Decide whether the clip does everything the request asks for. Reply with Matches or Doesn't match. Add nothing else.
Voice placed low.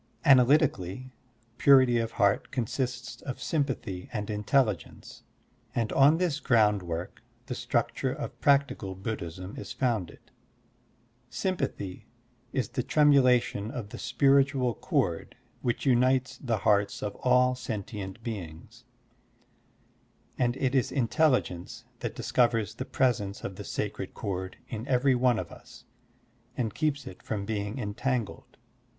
Matches